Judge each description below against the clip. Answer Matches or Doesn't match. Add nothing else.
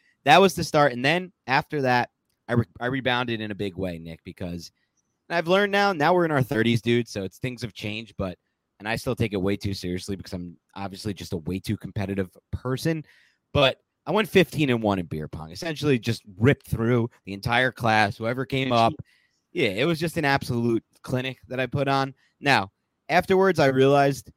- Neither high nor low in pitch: Doesn't match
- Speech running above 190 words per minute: Matches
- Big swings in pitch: Matches